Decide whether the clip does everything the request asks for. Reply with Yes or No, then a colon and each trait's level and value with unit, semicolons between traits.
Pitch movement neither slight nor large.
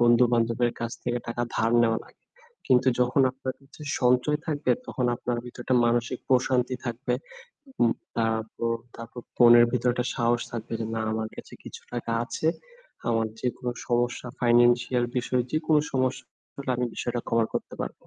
No: narrow, 1.3 semitones